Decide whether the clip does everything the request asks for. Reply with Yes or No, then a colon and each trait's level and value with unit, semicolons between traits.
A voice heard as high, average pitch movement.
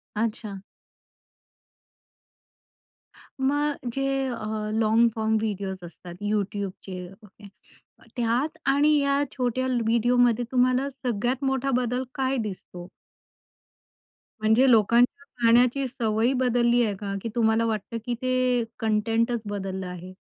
Yes: high, 235 Hz; average, 3.2 semitones